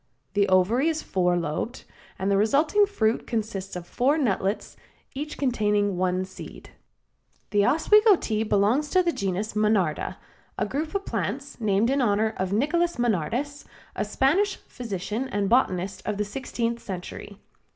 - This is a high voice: Yes, high, 220 Hz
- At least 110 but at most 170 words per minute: Yes, average, 150 wpm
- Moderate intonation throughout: No, wide, 6.0 semitones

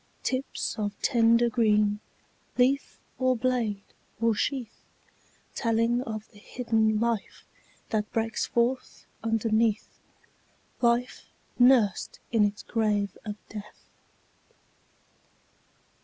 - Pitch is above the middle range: Yes, high, 225 Hz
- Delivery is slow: Yes, slow, 95 wpm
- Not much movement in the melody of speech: Yes, narrow, 2.2 semitones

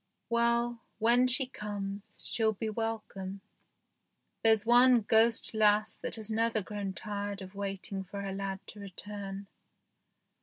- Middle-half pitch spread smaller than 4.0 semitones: Yes, narrow, 2.4 semitones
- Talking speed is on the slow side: Yes, slow, 130 wpm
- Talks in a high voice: Yes, high, 210 Hz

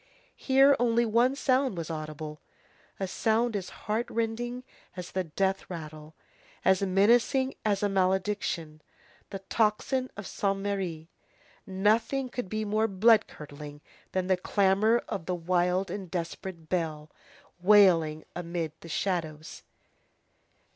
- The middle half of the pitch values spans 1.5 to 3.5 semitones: No, average, 4.7 semitones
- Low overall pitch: No, high, 190 Hz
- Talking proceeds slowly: Yes, slow, 125 wpm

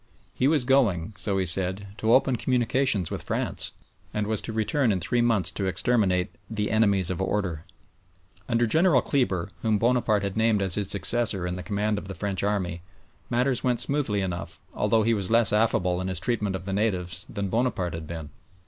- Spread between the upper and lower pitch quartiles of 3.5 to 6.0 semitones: Yes, average, 4.0 semitones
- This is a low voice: Yes, low, 105 Hz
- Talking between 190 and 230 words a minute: Yes, average, 195 wpm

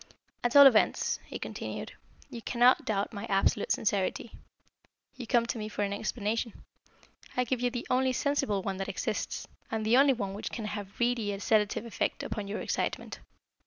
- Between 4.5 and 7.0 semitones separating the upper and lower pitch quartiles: No, average, 3.1 semitones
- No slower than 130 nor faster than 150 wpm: No, average, 180 wpm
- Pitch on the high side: Yes, high, 220 Hz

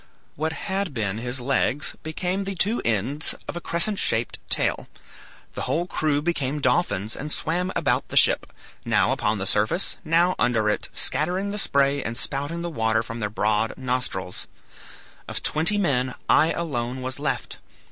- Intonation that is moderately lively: No, wide, 6.6 semitones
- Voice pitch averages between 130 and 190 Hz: Yes, medium, 140 Hz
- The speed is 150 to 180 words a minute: Yes, average, 165 wpm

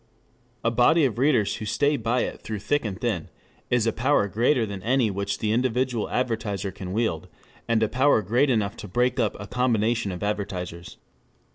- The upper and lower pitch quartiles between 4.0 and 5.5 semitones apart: No, average, 3.5 semitones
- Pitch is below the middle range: Yes, low, 110 Hz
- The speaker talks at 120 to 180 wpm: No, average, 190 wpm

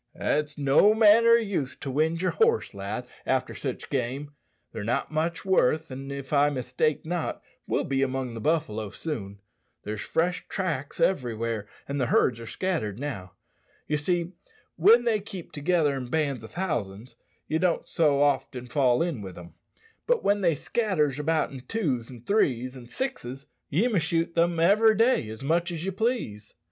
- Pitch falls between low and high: Yes, medium, 145 Hz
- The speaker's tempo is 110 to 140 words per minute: No, average, 175 wpm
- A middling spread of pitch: No, wide, 5.9 semitones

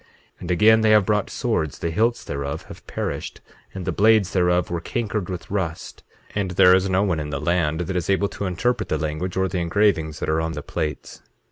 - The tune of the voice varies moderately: Yes, average, 3.9 semitones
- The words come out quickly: Yes, fast, 225 wpm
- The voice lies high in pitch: No, very low, 90 Hz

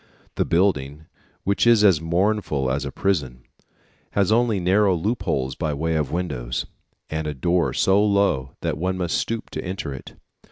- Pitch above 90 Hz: No, very low, 85 Hz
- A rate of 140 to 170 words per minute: Yes, average, 165 wpm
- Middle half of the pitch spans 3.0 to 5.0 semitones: No, wide, 5.4 semitones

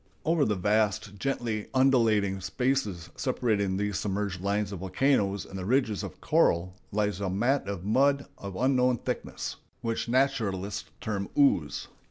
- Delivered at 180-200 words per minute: No, average, 145 wpm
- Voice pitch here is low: Yes, low, 105 Hz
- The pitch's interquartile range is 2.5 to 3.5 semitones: No, average, 4.6 semitones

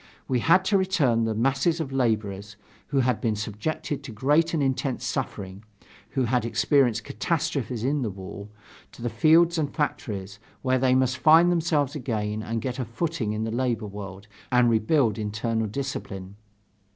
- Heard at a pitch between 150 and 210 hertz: No, low, 125 Hz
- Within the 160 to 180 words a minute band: Yes, average, 165 wpm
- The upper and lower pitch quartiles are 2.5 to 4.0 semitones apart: No, average, 5.1 semitones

